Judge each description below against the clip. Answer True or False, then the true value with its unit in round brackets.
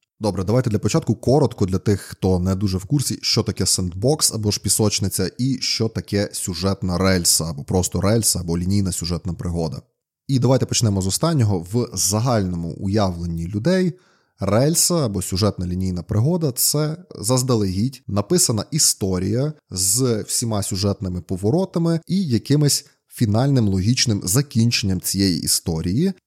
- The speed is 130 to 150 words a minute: True (135 wpm)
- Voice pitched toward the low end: True (105 Hz)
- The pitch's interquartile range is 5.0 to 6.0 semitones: True (5.5 semitones)